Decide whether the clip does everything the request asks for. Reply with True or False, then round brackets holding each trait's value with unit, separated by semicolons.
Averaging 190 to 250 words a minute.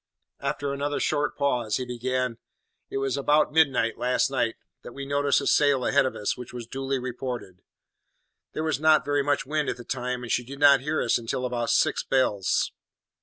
True (195 wpm)